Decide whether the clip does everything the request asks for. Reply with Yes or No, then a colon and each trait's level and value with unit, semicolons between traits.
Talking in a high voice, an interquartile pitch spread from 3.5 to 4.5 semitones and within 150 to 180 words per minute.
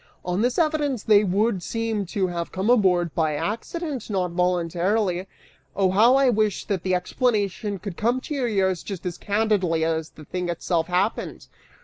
Yes: high, 195 Hz; average, 3.9 semitones; average, 170 wpm